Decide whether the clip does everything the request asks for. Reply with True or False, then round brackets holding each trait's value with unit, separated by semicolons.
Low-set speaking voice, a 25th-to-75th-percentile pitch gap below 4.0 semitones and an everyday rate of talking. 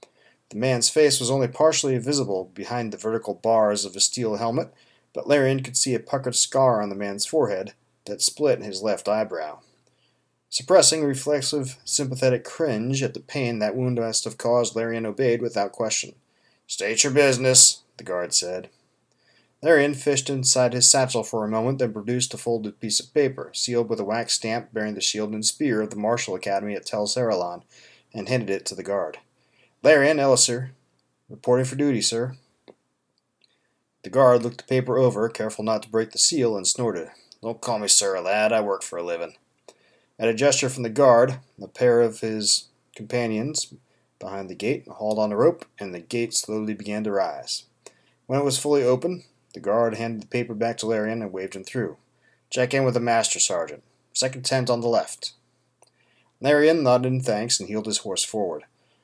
True (120 Hz; 3.3 semitones; 185 wpm)